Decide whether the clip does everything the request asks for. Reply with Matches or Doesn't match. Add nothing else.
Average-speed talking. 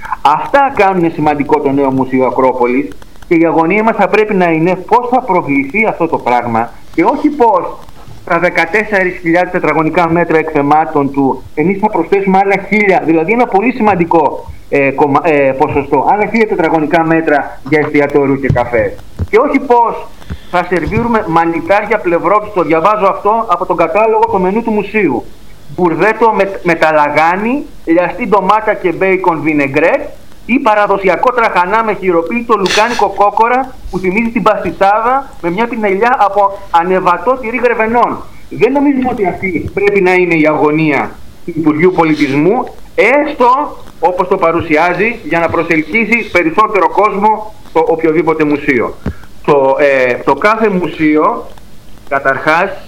Matches